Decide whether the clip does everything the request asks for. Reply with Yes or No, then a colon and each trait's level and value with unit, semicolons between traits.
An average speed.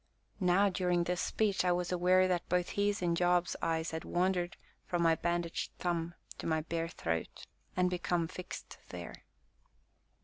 Yes: average, 160 wpm